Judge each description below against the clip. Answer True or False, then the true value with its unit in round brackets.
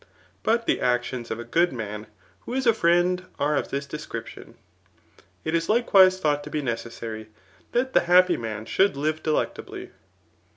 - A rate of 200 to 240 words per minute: False (170 wpm)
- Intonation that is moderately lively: False (7.4 semitones)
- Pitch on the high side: False (150 Hz)